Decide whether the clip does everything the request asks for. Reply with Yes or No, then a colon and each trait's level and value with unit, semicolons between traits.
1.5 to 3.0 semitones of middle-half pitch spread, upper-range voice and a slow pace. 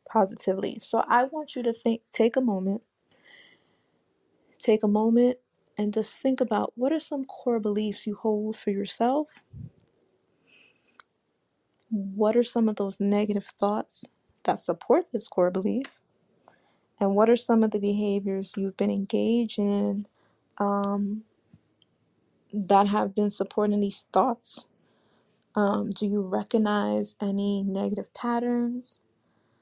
Yes: average, 2.7 semitones; high, 210 Hz; slow, 130 wpm